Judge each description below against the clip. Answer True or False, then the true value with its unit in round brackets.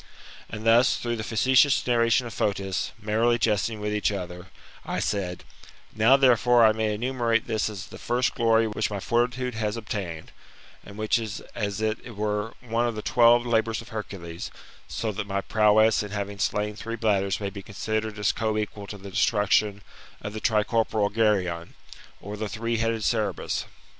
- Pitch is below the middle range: True (110 Hz)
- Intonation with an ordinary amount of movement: False (2.0 semitones)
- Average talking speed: True (175 wpm)